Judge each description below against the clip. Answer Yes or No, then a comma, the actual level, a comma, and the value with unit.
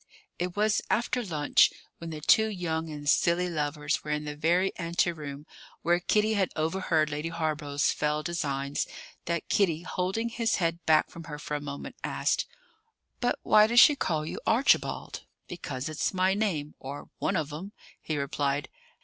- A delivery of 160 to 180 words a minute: Yes, average, 170 wpm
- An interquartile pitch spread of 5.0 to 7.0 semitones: No, average, 3.9 semitones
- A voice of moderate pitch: Yes, medium, 165 Hz